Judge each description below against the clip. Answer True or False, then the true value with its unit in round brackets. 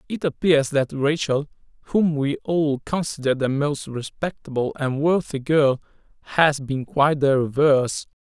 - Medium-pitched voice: True (145 Hz)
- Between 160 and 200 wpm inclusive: False (140 wpm)